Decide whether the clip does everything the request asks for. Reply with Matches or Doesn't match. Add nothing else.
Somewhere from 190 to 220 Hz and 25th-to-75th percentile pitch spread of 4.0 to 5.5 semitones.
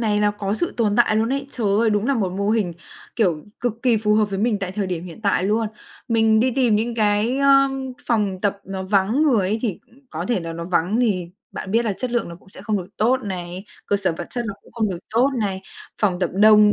Doesn't match